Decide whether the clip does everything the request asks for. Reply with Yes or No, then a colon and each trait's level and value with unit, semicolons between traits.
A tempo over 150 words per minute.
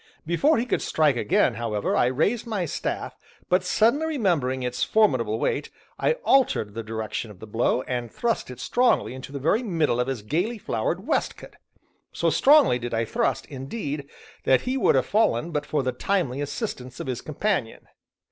Yes: average, 180 wpm